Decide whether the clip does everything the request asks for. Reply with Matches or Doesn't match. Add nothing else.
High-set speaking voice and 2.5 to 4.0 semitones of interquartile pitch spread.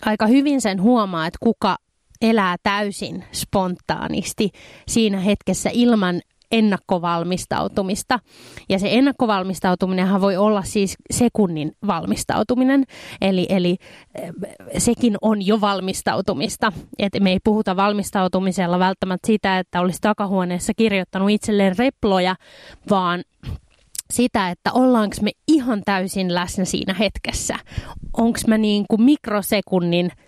Matches